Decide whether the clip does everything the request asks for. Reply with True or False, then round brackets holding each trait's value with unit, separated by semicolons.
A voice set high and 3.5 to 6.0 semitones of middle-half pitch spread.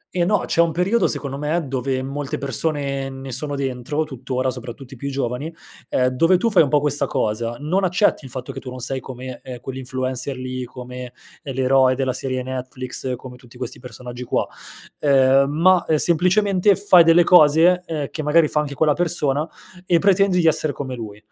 False (135 Hz; 4.1 semitones)